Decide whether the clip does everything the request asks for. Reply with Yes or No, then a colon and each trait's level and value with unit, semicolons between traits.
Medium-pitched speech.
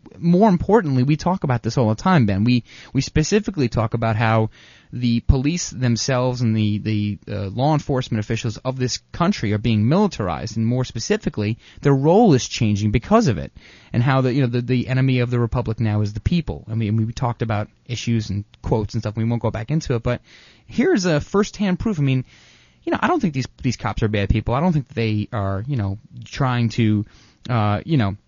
No: low, 120 Hz